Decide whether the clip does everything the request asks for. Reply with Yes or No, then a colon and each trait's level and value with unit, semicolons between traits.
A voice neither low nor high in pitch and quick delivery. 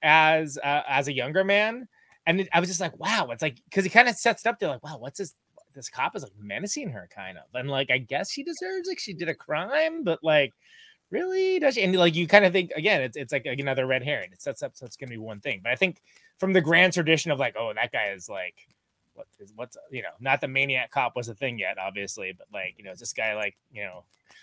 Yes: medium, 165 Hz; fast, 280 wpm